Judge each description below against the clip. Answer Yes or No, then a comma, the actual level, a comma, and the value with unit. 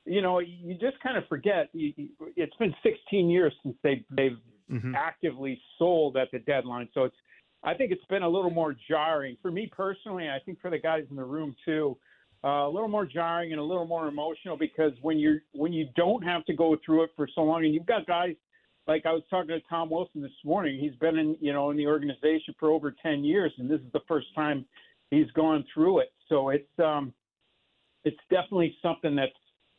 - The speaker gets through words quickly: Yes, fast, 215 wpm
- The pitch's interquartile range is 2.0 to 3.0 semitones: No, average, 3.5 semitones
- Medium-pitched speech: Yes, medium, 160 Hz